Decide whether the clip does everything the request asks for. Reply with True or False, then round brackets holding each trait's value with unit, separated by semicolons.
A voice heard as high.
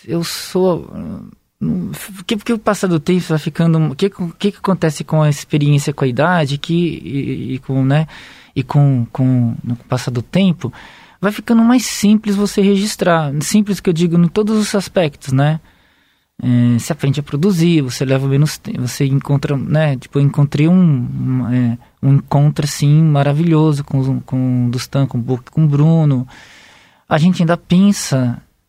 False (155 Hz)